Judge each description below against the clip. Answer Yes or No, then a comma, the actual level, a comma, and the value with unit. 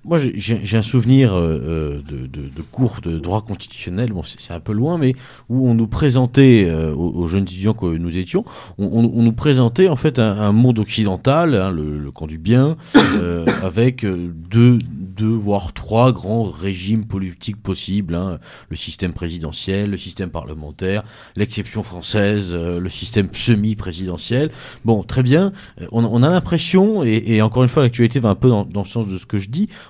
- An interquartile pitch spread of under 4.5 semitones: No, average, 5.1 semitones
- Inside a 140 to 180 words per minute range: No, average, 195 wpm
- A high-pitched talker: No, low, 105 Hz